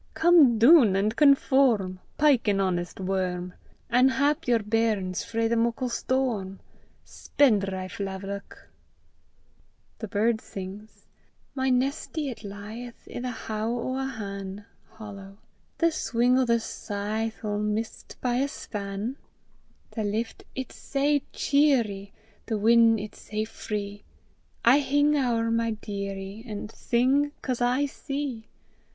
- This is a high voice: Yes, high, 225 Hz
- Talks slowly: Yes, slow, 130 wpm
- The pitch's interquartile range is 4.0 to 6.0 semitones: Yes, average, 4.3 semitones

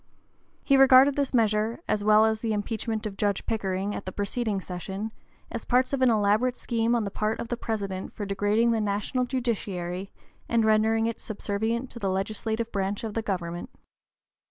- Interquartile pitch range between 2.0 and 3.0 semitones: Yes, narrow, 2.6 semitones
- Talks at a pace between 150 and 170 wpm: No, average, 180 wpm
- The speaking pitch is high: Yes, high, 215 Hz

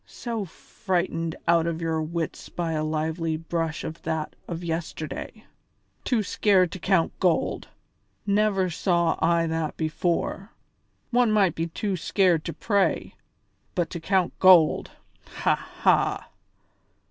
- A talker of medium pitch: Yes, medium, 170 Hz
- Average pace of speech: No, slow, 130 wpm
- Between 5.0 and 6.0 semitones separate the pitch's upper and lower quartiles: No, average, 2.8 semitones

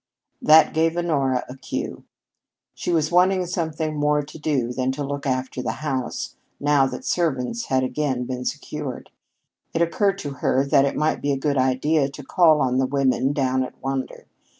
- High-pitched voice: No, medium, 140 Hz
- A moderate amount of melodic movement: Yes, average, 3.1 semitones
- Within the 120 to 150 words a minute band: No, average, 180 wpm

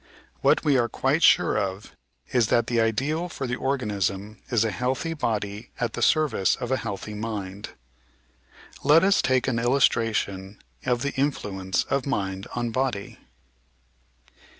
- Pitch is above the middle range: No, low, 115 Hz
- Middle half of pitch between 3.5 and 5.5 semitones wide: Yes, average, 4.5 semitones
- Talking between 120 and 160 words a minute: Yes, average, 150 wpm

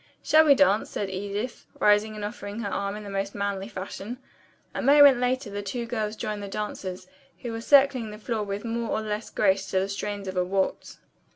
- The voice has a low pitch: No, high, 210 Hz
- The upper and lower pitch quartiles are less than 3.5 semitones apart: Yes, average, 2.7 semitones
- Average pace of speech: No, fast, 210 wpm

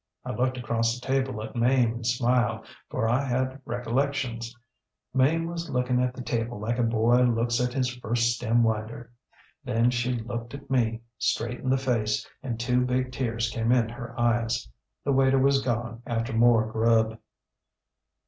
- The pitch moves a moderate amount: No, narrow, 1.8 semitones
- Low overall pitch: Yes, low, 120 Hz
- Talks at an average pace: Yes, average, 170 wpm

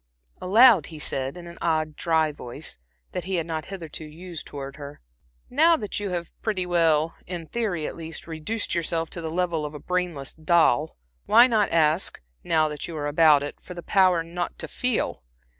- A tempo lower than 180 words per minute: No, average, 190 wpm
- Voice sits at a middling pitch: Yes, medium, 165 Hz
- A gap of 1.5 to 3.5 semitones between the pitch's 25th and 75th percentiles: Yes, average, 2.8 semitones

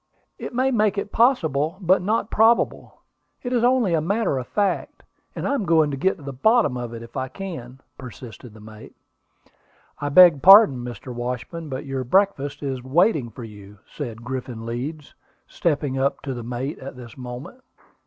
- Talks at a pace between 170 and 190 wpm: Yes, average, 185 wpm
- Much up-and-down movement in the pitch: Yes, wide, 7.5 semitones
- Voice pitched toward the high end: No, medium, 140 Hz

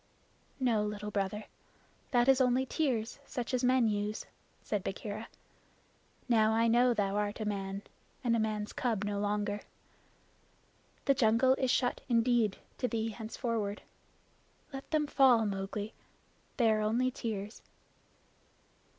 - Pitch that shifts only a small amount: No, average, 3.0 semitones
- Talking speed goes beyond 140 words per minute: No, slow, 135 wpm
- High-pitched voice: Yes, high, 220 Hz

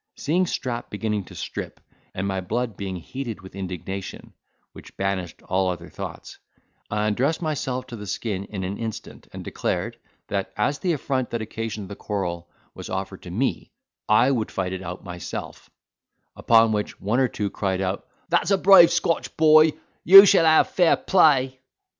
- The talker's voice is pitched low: Yes, low, 110 Hz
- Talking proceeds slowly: No, average, 170 wpm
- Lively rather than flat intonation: Yes, wide, 6.2 semitones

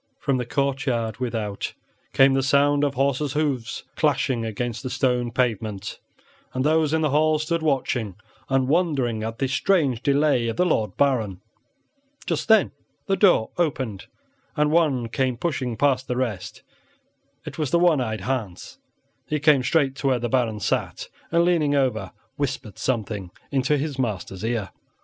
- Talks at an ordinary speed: Yes, average, 160 wpm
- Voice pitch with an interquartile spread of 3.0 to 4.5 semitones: Yes, average, 4.2 semitones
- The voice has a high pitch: No, low, 130 Hz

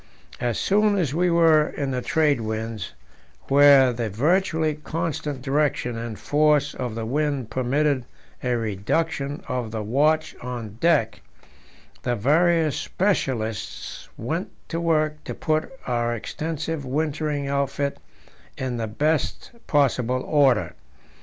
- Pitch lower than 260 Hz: Yes, medium, 140 Hz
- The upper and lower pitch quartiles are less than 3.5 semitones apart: No, average, 4.3 semitones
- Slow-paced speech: Yes, slow, 125 wpm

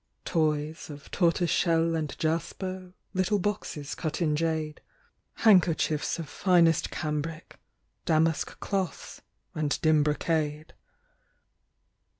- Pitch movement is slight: Yes, narrow, 2.3 semitones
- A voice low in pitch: No, medium, 160 Hz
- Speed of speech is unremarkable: No, slow, 95 wpm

